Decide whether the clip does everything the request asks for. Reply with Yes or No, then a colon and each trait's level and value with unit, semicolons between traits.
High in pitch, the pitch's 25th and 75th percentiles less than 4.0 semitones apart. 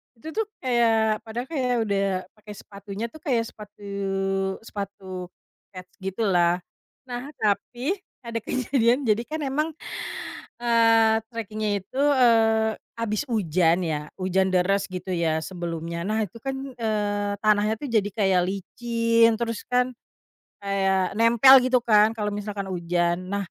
Yes: high, 215 Hz; average, 3.3 semitones